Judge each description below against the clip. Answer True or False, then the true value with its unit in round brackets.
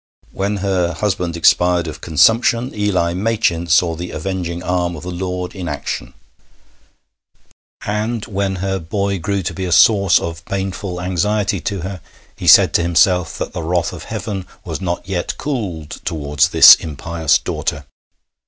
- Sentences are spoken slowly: False (155 wpm)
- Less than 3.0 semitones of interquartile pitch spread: True (2.6 semitones)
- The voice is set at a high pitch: False (90 Hz)